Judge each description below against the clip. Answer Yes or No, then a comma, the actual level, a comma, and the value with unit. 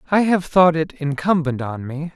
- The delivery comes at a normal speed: Yes, average, 195 wpm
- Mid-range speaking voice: Yes, medium, 160 Hz